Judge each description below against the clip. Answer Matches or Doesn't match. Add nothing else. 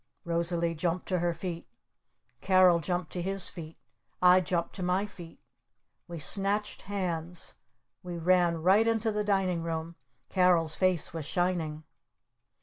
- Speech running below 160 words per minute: Matches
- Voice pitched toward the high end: Doesn't match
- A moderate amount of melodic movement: Doesn't match